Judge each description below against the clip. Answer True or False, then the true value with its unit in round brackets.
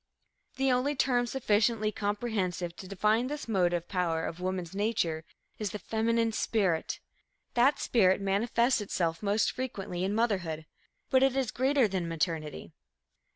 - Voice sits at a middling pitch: False (205 Hz)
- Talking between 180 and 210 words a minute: False (140 wpm)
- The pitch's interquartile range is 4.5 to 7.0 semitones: True (4.9 semitones)